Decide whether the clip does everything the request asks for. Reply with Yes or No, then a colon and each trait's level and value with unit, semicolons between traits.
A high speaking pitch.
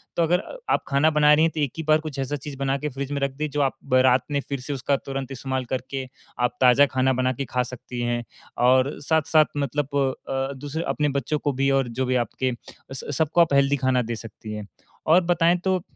No: medium, 140 Hz